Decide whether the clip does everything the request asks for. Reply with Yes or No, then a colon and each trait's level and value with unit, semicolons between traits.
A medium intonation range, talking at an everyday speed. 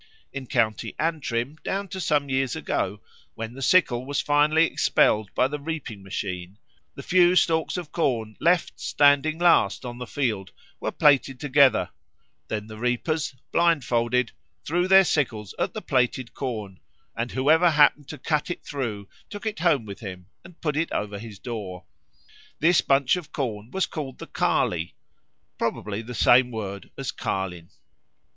No: wide, 6.1 semitones; average, 160 wpm